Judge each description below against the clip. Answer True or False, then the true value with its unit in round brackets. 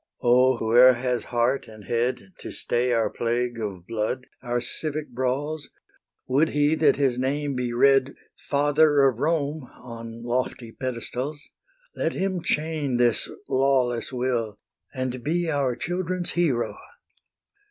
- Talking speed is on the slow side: True (130 wpm)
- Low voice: True (130 Hz)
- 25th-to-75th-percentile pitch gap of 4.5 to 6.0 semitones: False (3.4 semitones)